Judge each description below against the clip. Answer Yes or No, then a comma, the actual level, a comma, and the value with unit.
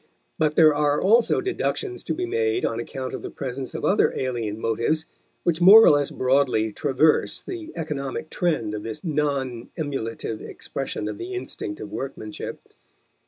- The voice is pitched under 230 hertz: Yes, medium, 140 Hz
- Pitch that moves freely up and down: Yes, wide, 5.9 semitones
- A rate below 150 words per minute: No, average, 165 wpm